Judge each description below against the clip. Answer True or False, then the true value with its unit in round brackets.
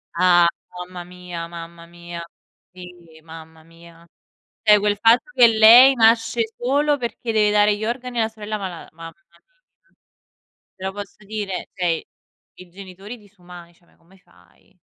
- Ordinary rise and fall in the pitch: True (4.3 semitones)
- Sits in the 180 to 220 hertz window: True (190 Hz)